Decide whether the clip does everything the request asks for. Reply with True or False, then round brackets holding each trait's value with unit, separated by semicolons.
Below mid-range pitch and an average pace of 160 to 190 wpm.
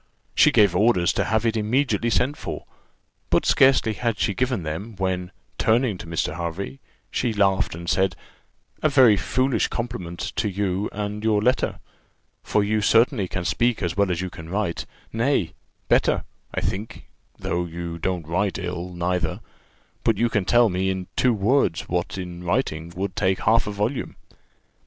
True (100 Hz; 170 wpm)